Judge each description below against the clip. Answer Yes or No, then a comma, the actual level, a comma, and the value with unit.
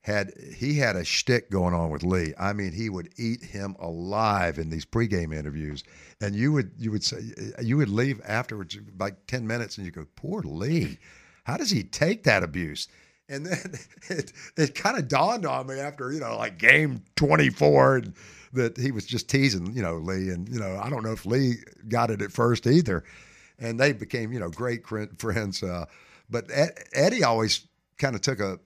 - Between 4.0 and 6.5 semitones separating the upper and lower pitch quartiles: Yes, average, 4.9 semitones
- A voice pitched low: Yes, low, 110 Hz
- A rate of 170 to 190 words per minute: No, average, 200 wpm